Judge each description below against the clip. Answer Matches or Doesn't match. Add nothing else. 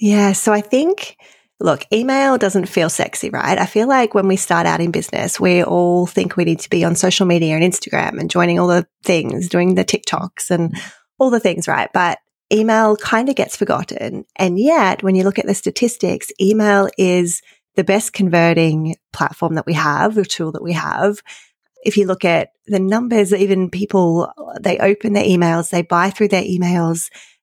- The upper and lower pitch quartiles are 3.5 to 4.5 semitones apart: Doesn't match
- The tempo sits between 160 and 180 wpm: Doesn't match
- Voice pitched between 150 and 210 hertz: Matches